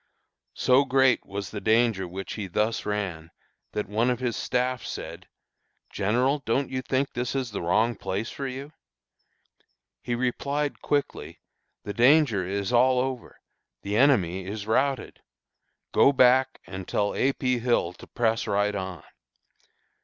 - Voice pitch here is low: Yes, low, 120 Hz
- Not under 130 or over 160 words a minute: Yes, average, 145 wpm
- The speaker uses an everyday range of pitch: Yes, average, 4.3 semitones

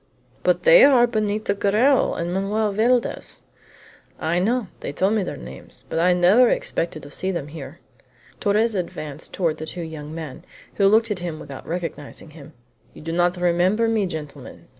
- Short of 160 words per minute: No, average, 175 wpm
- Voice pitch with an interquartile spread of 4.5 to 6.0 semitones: Yes, average, 5.1 semitones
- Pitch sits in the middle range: Yes, medium, 180 Hz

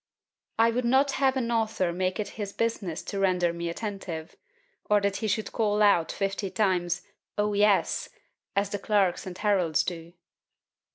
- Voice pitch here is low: No, high, 200 Hz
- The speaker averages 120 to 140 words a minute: No, average, 165 wpm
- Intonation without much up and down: No, average, 3.2 semitones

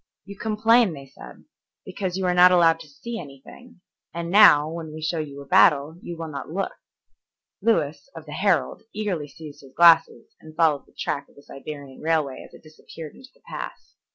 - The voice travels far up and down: No, average, 3.9 semitones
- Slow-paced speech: No, average, 195 wpm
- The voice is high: No, medium, 165 Hz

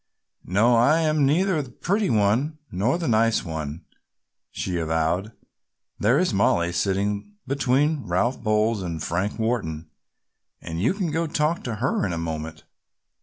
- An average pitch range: No, wide, 8.7 semitones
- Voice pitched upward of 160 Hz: No, low, 110 Hz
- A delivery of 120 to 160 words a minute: Yes, average, 150 wpm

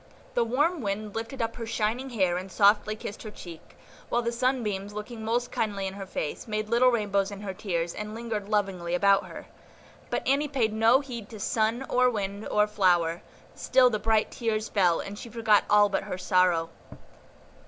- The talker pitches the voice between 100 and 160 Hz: No, high, 215 Hz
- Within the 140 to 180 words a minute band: No, average, 190 wpm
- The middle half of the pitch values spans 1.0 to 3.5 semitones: Yes, average, 3.0 semitones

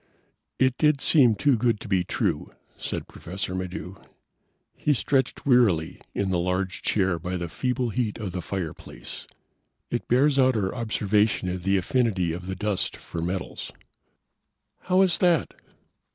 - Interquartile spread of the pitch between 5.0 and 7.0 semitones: Yes, wide, 5.6 semitones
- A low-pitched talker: Yes, low, 100 Hz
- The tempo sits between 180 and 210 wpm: No, average, 150 wpm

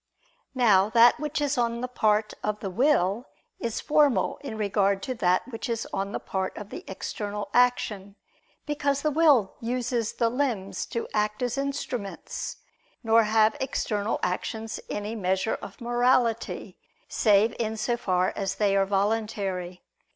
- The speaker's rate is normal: Yes, average, 150 wpm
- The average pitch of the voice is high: Yes, high, 220 Hz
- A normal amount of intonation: Yes, average, 3.6 semitones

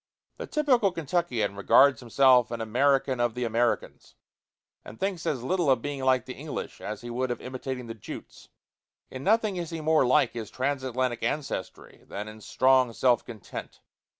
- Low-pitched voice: Yes, low, 130 Hz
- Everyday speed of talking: Yes, average, 170 wpm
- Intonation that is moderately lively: Yes, average, 3.5 semitones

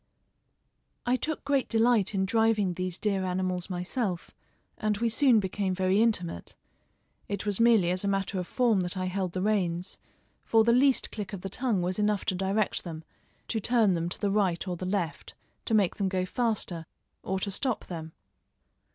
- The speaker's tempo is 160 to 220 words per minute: Yes, average, 185 wpm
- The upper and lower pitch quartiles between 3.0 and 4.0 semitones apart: Yes, average, 3.3 semitones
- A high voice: Yes, high, 195 Hz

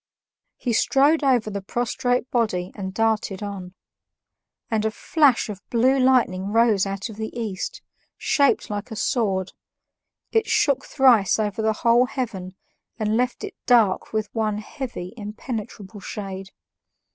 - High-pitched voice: Yes, high, 220 Hz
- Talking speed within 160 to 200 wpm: No, average, 140 wpm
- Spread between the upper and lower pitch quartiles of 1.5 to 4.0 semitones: Yes, average, 3.6 semitones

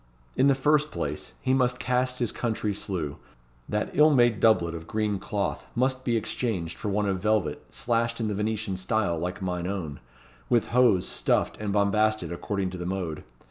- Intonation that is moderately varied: Yes, average, 4.5 semitones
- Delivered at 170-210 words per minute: Yes, average, 180 wpm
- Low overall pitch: Yes, low, 105 Hz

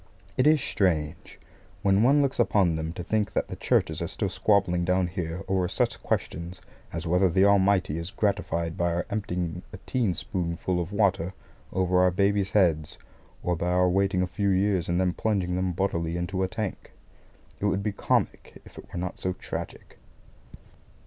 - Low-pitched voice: Yes, very low, 90 Hz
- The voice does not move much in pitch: Yes, narrow, 2.3 semitones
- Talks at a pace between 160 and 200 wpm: Yes, average, 185 wpm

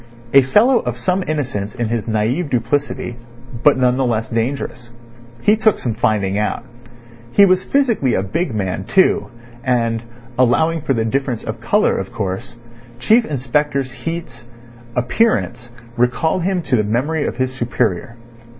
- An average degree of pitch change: No, wide, 5.7 semitones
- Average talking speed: Yes, average, 150 wpm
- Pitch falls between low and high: No, low, 125 Hz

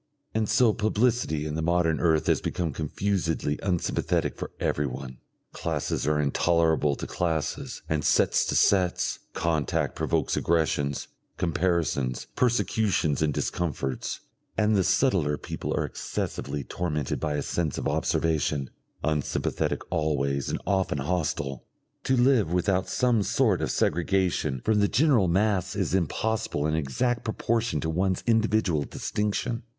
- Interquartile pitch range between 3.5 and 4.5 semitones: No, wide, 5.5 semitones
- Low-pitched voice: Yes, very low, 85 Hz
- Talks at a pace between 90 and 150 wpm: Yes, slow, 135 wpm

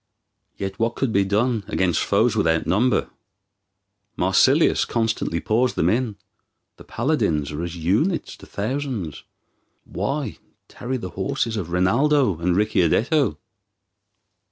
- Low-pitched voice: Yes, low, 105 Hz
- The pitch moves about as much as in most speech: No, wide, 6.0 semitones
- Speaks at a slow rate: Yes, slow, 120 wpm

